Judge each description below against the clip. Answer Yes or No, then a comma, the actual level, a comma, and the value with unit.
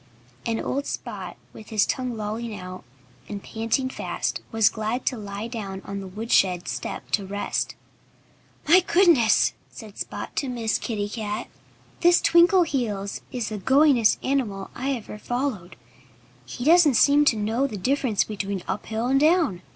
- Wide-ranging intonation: No, average, 4.7 semitones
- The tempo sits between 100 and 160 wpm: Yes, average, 150 wpm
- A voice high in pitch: Yes, high, 225 Hz